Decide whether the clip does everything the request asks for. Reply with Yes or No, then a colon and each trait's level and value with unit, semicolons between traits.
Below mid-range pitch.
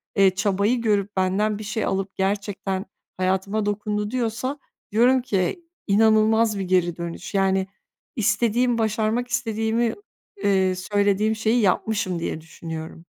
No: high, 205 Hz